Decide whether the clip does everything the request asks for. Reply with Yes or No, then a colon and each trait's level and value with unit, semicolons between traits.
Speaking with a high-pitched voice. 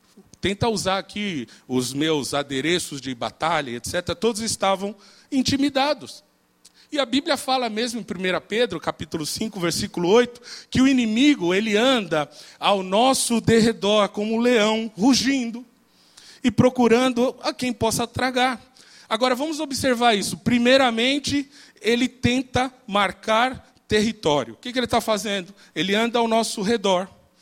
Yes: high, 225 Hz